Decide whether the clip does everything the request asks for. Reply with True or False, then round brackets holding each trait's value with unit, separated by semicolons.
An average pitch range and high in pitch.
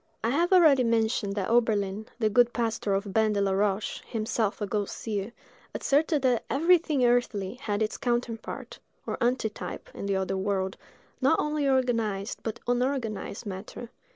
True (3.6 semitones; 225 Hz)